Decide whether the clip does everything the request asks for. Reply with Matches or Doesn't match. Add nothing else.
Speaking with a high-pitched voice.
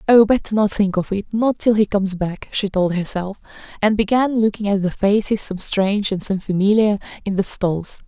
Matches